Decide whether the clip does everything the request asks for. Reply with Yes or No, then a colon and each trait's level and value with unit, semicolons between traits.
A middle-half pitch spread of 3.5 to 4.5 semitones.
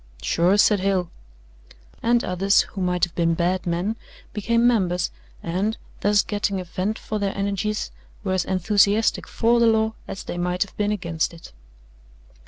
No: average, 2.9 semitones